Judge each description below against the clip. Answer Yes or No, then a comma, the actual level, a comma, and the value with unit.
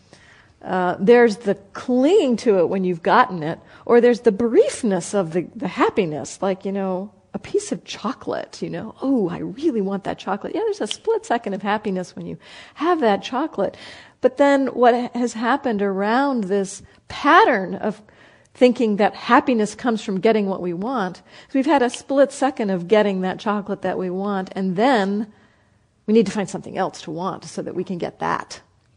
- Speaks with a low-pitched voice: No, high, 210 Hz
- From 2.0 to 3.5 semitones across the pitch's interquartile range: No, average, 4.7 semitones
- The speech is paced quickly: No, average, 190 wpm